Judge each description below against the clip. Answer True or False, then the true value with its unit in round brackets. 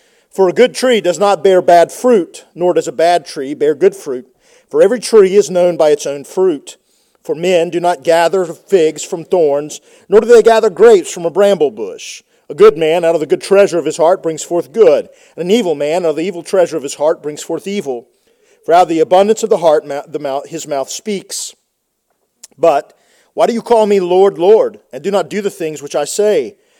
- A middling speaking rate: False (230 wpm)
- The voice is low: False (195 Hz)